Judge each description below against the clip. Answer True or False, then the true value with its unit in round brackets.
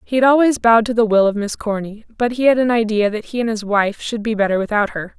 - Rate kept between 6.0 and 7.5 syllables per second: True (6.3 syllables/s)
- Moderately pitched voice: False (220 Hz)